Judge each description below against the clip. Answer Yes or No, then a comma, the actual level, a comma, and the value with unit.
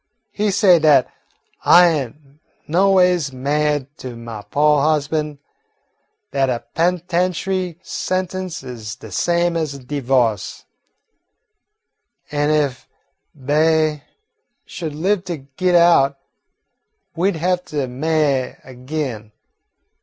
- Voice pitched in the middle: Yes, medium, 150 Hz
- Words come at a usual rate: No, slow, 105 wpm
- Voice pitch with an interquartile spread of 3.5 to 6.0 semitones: Yes, average, 4.5 semitones